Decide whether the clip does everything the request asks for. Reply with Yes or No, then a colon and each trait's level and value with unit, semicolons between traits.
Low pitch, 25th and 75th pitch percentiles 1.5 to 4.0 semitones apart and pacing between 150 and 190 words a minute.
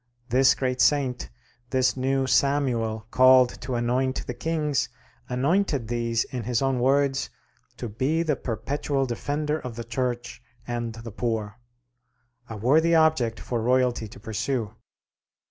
No: low, 125 Hz; narrow, 2.6 semitones; slow, 135 wpm